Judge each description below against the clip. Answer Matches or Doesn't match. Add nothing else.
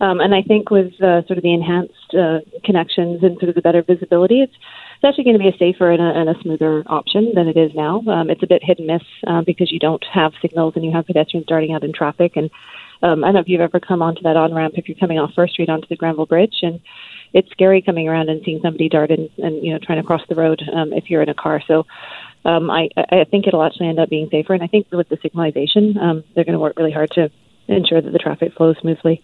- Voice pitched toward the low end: Doesn't match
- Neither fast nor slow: Doesn't match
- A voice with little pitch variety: Matches